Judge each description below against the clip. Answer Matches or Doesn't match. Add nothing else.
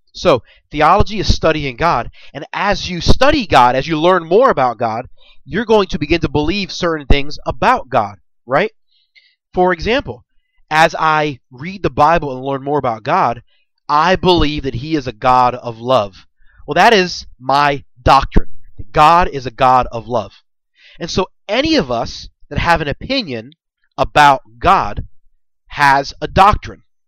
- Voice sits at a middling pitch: Matches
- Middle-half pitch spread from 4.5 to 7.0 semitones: Matches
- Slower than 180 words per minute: Matches